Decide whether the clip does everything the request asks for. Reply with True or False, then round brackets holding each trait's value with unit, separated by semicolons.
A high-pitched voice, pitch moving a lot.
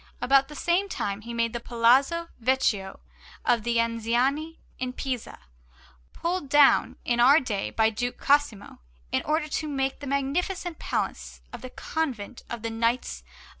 False (255 Hz; 4.2 semitones)